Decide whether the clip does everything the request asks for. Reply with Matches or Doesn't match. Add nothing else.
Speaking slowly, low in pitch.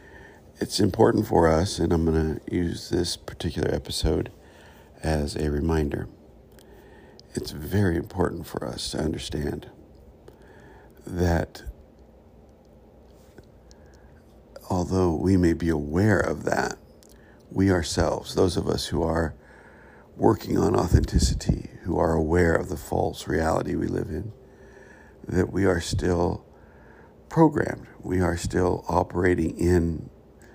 Matches